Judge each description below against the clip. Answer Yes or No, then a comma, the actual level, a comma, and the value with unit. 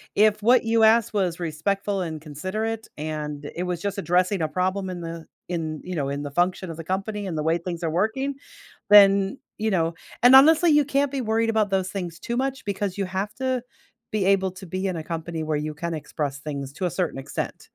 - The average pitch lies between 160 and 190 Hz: Yes, medium, 185 Hz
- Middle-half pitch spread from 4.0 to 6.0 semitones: Yes, average, 4.6 semitones